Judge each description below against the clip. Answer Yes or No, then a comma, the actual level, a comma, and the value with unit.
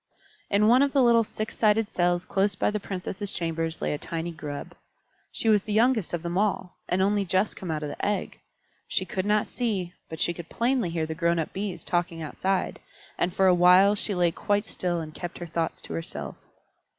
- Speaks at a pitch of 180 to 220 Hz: Yes, medium, 185 Hz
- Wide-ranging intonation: No, average, 3.5 semitones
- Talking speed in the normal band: No, fast, 220 wpm